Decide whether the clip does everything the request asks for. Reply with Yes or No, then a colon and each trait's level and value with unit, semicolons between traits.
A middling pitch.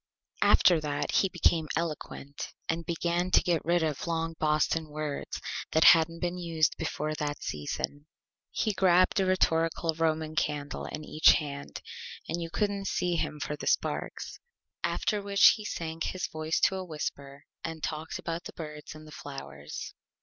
Yes: medium, 160 Hz